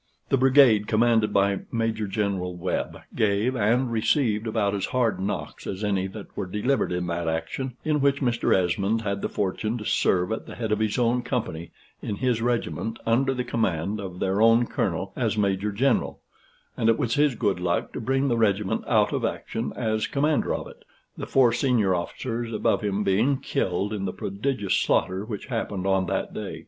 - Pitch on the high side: No, low, 110 Hz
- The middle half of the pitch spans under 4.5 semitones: Yes, average, 3.6 semitones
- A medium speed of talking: Yes, average, 190 wpm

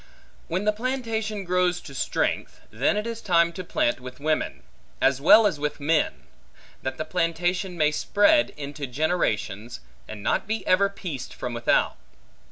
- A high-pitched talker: No, medium, 170 Hz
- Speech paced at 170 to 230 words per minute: No, average, 160 wpm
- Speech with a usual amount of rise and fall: No, wide, 6.3 semitones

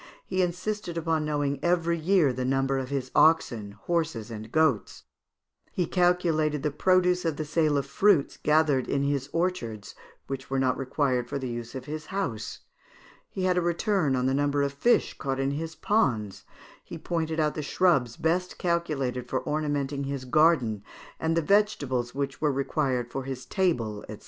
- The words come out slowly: No, average, 175 wpm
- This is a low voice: No, medium, 145 Hz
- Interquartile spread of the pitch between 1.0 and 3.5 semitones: No, average, 4.4 semitones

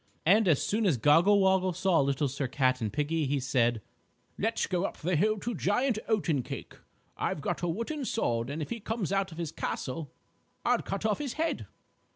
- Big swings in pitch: Yes, wide, 6.9 semitones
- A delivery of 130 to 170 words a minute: No, average, 195 wpm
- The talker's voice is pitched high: No, medium, 175 Hz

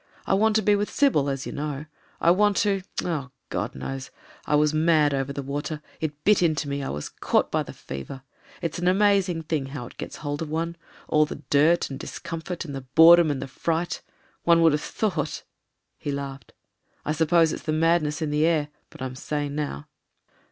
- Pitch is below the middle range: No, medium, 155 Hz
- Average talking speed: No, fast, 215 wpm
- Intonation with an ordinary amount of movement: Yes, average, 3.1 semitones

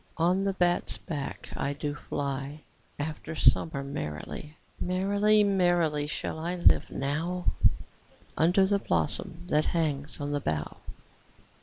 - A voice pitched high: No, medium, 155 Hz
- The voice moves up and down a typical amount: Yes, average, 3.9 semitones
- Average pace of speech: No, slow, 130 wpm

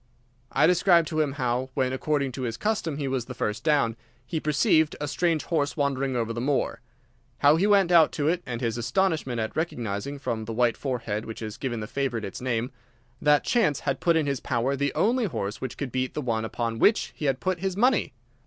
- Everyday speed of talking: No, fast, 220 wpm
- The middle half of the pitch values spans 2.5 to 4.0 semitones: No, average, 5.0 semitones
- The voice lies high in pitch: No, low, 135 Hz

